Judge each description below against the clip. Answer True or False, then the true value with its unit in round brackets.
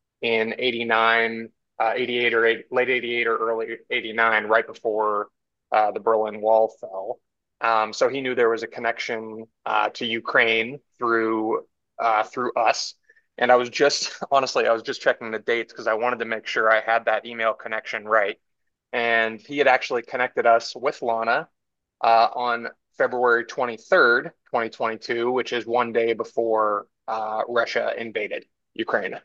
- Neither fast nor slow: True (160 wpm)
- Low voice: True (115 Hz)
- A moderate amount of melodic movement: False (1.3 semitones)